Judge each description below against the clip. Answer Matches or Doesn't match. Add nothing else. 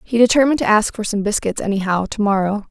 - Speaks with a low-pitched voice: Doesn't match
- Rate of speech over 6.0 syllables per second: Matches